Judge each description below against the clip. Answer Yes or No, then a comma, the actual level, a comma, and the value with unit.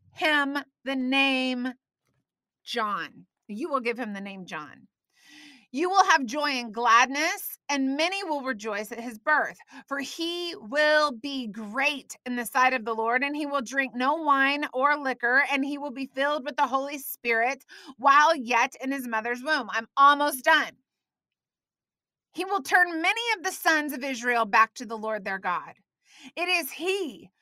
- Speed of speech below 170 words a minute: No, average, 175 wpm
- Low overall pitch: No, very high, 275 Hz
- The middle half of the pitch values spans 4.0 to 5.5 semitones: No, average, 3.6 semitones